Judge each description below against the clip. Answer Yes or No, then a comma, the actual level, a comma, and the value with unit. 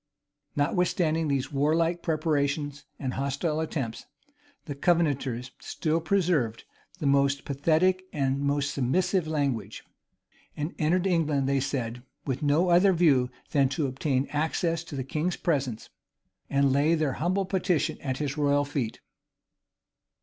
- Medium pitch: Yes, medium, 145 Hz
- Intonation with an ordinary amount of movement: Yes, average, 3.3 semitones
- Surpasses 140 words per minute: No, slow, 135 wpm